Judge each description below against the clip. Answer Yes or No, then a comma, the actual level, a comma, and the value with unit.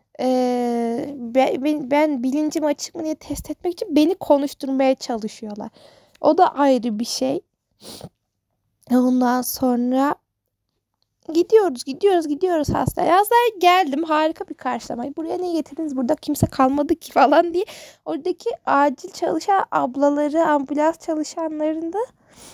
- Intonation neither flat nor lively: Yes, average, 4.0 semitones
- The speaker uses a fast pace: No, average, 125 wpm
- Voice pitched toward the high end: Yes, very high, 300 Hz